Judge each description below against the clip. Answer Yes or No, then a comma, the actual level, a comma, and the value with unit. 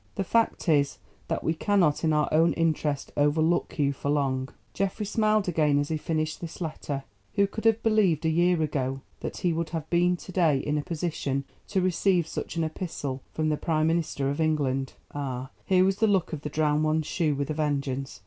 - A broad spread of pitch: No, average, 3.4 semitones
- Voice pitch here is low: No, medium, 155 Hz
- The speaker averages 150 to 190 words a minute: No, fast, 205 wpm